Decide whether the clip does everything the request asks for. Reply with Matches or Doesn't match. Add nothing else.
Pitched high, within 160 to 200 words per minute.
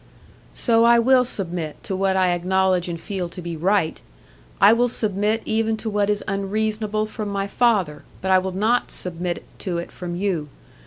Matches